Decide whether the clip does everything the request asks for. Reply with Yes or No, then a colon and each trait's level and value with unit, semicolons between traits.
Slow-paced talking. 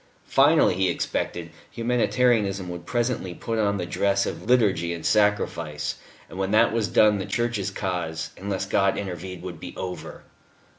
No: average, 155 wpm